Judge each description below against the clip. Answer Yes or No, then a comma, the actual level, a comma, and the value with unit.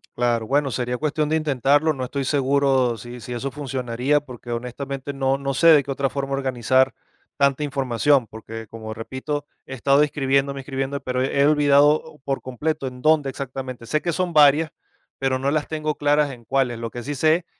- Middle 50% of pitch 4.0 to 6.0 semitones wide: No, narrow, 2.5 semitones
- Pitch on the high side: No, low, 135 Hz